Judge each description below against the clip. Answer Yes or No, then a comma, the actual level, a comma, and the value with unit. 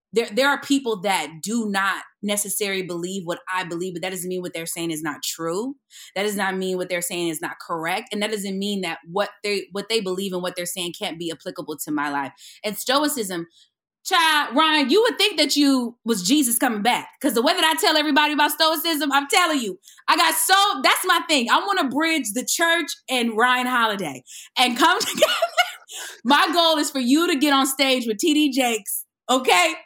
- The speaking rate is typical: No, fast, 215 wpm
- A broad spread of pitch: Yes, wide, 8.3 semitones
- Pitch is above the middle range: Yes, high, 235 Hz